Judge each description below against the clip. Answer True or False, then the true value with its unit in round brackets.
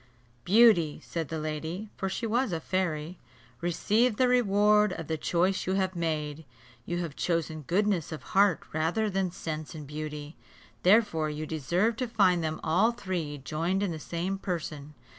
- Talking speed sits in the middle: True (165 wpm)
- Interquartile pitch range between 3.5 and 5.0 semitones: True (4.3 semitones)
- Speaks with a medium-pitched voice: True (175 Hz)